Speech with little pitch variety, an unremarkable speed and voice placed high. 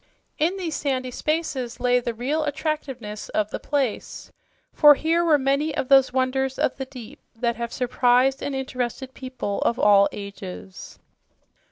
No: average, 3.3 semitones; average, 155 wpm; very high, 260 Hz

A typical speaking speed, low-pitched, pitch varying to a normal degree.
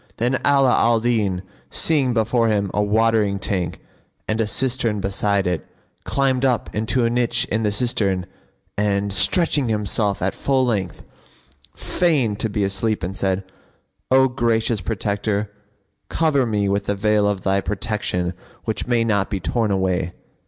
Yes: average, 150 wpm; low, 105 Hz; average, 3.3 semitones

